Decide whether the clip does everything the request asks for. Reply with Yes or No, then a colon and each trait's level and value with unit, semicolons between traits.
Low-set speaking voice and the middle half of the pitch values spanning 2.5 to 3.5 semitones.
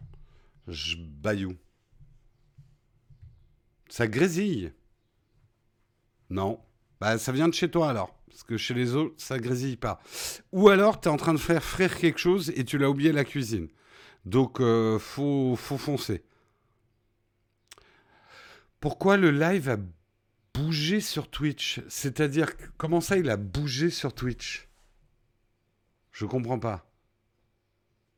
No: low, 125 Hz; average, 4.8 semitones